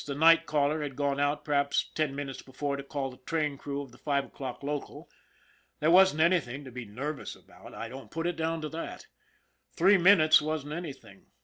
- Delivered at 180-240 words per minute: Yes, average, 200 wpm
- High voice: No, medium, 145 Hz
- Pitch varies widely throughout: No, narrow, 2.5 semitones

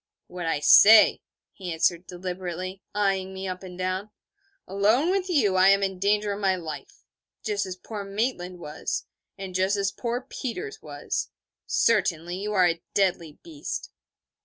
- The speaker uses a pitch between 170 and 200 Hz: Yes, high, 190 Hz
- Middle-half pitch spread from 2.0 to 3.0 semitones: Yes, narrow, 2.5 semitones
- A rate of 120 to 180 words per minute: Yes, average, 160 wpm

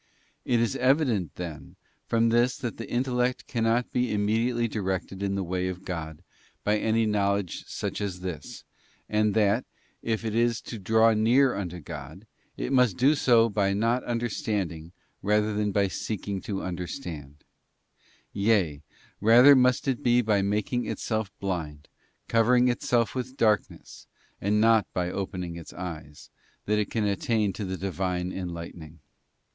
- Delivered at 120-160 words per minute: Yes, average, 155 wpm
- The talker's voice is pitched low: Yes, low, 105 Hz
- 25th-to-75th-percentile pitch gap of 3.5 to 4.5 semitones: Yes, average, 4.0 semitones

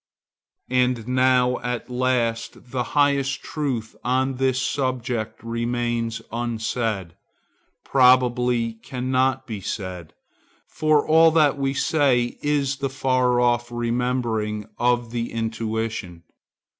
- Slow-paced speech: Yes, slow, 105 wpm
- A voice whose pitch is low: Yes, low, 125 Hz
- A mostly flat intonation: Yes, narrow, 2.2 semitones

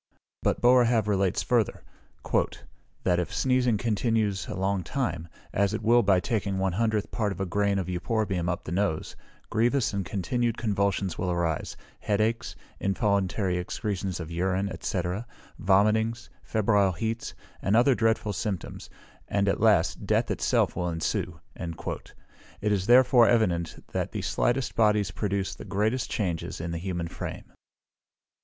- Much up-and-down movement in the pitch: No, average, 3.5 semitones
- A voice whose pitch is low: Yes, low, 100 Hz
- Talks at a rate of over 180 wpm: No, average, 150 wpm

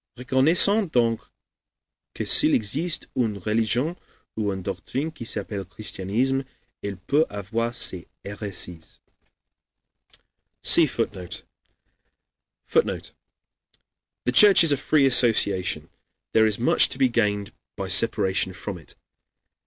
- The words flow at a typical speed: No, slow, 115 wpm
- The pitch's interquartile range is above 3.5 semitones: Yes, average, 5.0 semitones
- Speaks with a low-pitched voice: Yes, low, 115 Hz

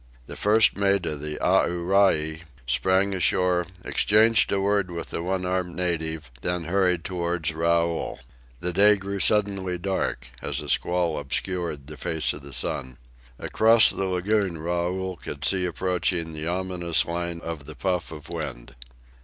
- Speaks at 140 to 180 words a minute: Yes, average, 155 wpm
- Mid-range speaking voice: No, very low, 90 Hz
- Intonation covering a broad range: No, narrow, 2.6 semitones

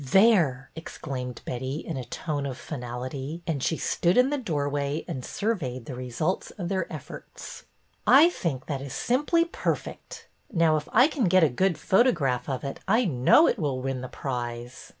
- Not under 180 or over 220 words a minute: Yes, average, 190 wpm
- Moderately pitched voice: Yes, medium, 145 Hz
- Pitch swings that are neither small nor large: No, wide, 6.5 semitones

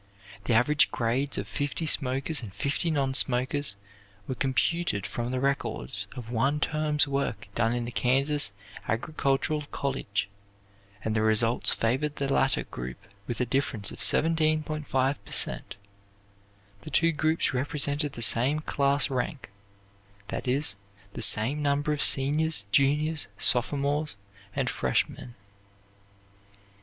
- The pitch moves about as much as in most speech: Yes, average, 4.0 semitones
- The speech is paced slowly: Yes, slow, 130 wpm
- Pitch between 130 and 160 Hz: Yes, low, 135 Hz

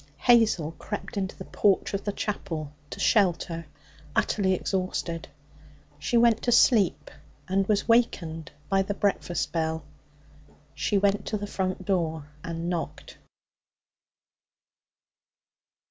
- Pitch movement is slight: No, average, 3.6 semitones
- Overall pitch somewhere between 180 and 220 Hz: Yes, high, 190 Hz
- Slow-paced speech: Yes, slow, 115 wpm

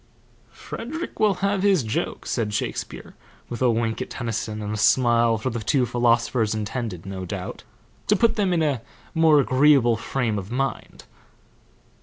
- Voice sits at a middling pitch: No, low, 120 Hz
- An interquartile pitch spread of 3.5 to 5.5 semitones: Yes, average, 5.2 semitones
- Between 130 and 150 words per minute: No, average, 165 wpm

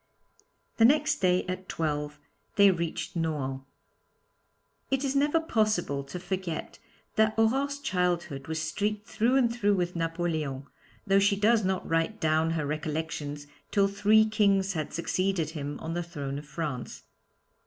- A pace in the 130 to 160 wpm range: Yes, average, 145 wpm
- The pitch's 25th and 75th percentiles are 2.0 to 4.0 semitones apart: No, average, 5.2 semitones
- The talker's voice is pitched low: No, medium, 180 Hz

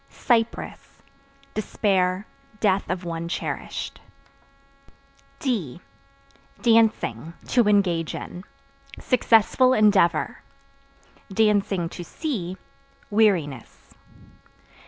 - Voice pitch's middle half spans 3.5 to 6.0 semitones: Yes, average, 4.4 semitones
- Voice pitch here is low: No, high, 195 Hz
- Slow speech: Yes, slow, 65 wpm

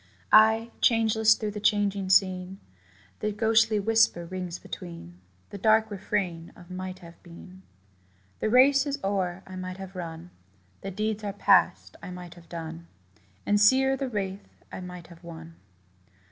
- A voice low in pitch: No, high, 190 Hz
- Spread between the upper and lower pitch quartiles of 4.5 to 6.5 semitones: No, average, 3.5 semitones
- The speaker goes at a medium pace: Yes, average, 155 wpm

